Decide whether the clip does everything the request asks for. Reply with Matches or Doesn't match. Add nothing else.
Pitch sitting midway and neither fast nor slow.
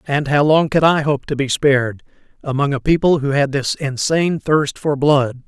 Doesn't match